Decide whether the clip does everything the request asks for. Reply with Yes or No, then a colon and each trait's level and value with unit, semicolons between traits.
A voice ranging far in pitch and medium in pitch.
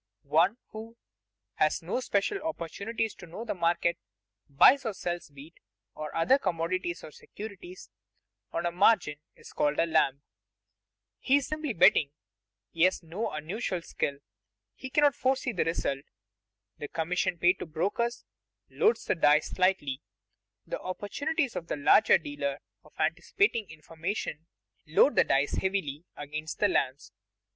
Yes: wide, 6.5 semitones; medium, 175 Hz